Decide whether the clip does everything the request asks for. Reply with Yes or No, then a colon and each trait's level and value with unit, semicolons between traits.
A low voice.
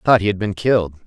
Yes: low, 100 Hz